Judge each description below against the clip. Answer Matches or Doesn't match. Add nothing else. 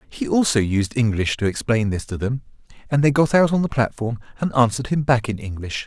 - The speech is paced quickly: Matches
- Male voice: Matches